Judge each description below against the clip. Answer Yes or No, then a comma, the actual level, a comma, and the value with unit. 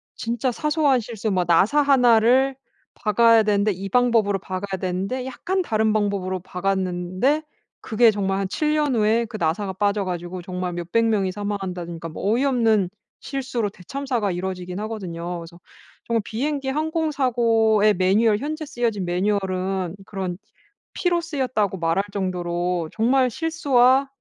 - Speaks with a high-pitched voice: Yes, high, 210 Hz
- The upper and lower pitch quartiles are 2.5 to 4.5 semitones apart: No, average, 5.2 semitones